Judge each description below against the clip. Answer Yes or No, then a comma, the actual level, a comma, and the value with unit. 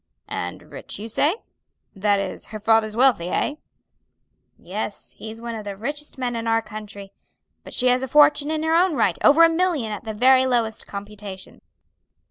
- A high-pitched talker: Yes, high, 230 Hz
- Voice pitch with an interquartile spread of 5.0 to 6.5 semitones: Yes, average, 5.3 semitones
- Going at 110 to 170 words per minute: No, average, 180 wpm